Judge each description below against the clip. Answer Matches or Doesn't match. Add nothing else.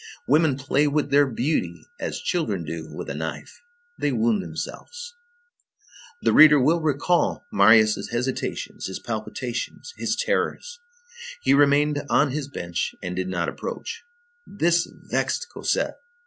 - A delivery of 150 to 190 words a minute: Doesn't match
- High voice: Doesn't match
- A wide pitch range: Matches